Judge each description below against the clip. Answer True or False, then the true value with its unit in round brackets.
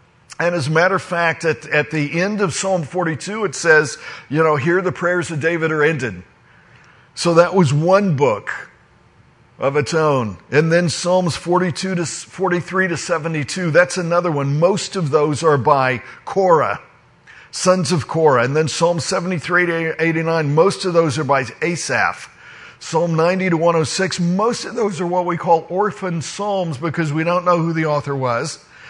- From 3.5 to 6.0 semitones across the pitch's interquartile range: False (3.0 semitones)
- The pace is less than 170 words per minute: False (180 wpm)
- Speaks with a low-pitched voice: False (165 Hz)